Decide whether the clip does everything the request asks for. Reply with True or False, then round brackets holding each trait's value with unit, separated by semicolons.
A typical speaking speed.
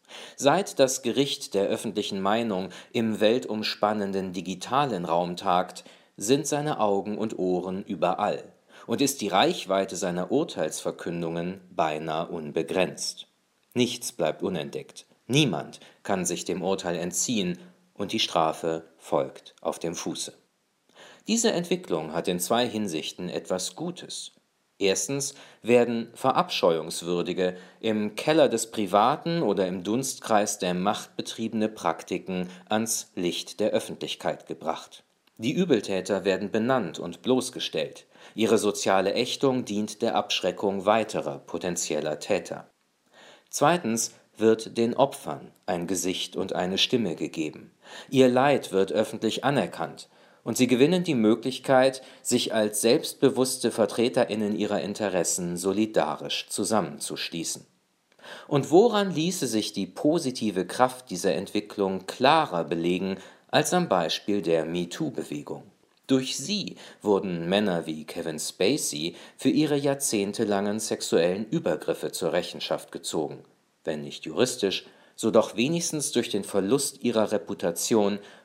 False (120 wpm)